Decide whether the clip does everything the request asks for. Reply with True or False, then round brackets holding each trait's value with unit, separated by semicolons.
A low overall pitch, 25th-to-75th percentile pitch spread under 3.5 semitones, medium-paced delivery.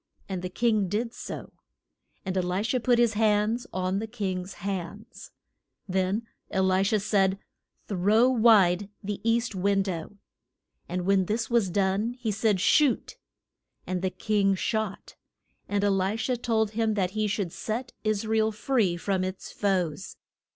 False (205 Hz; 2.8 semitones; 165 wpm)